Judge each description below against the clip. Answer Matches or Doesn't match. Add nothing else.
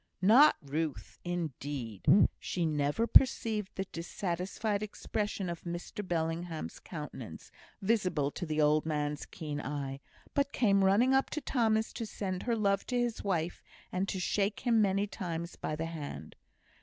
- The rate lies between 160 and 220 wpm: Doesn't match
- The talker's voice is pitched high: Doesn't match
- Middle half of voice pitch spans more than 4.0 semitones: Matches